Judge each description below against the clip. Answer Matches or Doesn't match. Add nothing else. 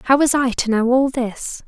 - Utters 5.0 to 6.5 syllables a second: Doesn't match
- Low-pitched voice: Doesn't match